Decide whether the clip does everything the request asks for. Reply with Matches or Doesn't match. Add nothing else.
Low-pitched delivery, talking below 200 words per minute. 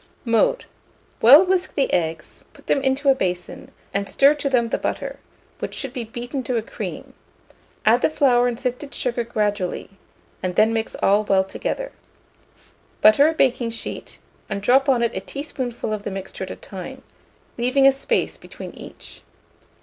Doesn't match